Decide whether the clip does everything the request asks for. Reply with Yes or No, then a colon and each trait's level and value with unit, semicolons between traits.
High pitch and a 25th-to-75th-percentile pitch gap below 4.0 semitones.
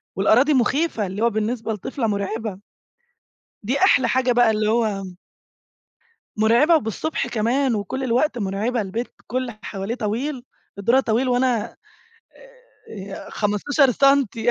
Yes: high, 235 Hz; average, 3.5 semitones